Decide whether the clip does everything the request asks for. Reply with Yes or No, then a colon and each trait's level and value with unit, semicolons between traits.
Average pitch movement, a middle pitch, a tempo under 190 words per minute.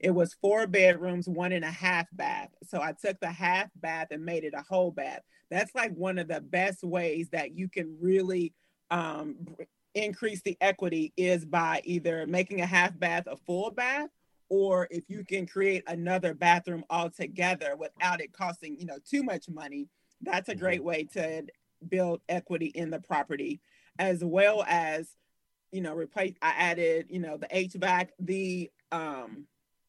No: narrow, 2.1 semitones; medium, 180 Hz; average, 175 wpm